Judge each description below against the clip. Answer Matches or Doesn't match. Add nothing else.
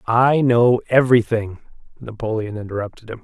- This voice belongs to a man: Matches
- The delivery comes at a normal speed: Doesn't match